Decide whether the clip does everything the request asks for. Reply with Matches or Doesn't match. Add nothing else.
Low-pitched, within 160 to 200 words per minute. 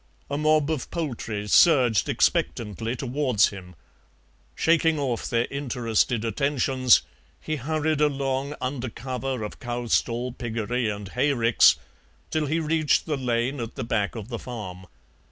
Doesn't match